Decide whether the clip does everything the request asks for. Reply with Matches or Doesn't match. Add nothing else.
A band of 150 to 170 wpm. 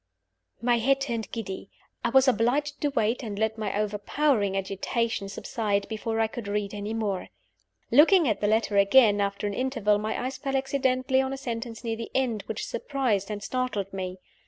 Doesn't match